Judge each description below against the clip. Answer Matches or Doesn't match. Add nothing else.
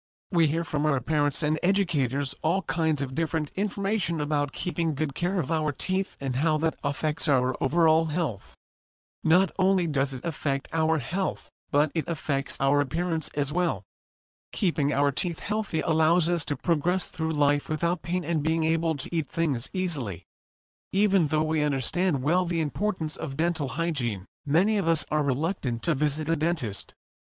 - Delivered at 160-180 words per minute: Matches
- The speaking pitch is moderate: Matches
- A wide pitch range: Doesn't match